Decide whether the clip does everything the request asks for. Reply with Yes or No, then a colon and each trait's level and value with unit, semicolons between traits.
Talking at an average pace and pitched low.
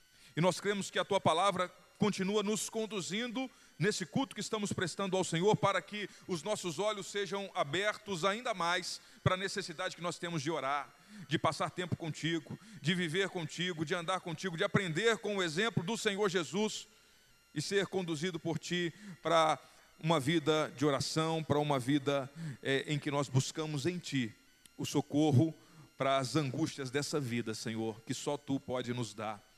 No: average, 170 wpm; medium, 170 Hz